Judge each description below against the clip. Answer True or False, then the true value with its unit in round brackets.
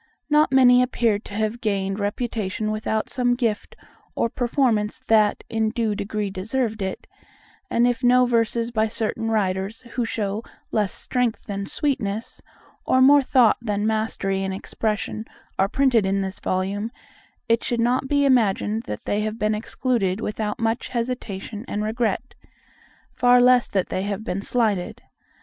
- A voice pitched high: True (220 Hz)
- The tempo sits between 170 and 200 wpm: False (155 wpm)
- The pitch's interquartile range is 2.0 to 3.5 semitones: True (3.0 semitones)